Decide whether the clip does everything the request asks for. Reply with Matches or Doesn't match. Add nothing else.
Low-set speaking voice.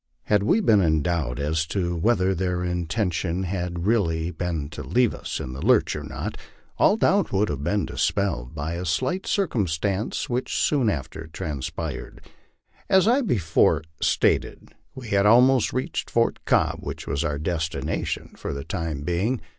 Matches